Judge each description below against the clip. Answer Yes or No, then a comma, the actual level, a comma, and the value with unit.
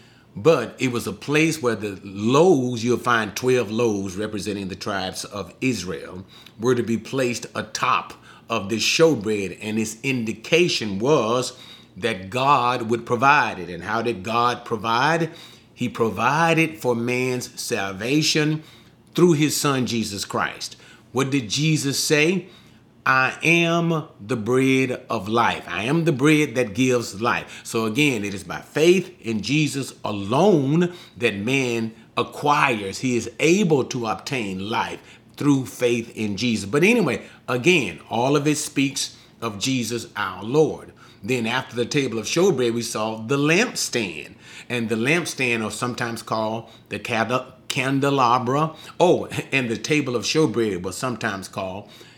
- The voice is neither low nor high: No, low, 120 Hz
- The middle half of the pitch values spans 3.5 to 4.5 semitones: Yes, average, 4.0 semitones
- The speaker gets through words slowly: No, average, 145 wpm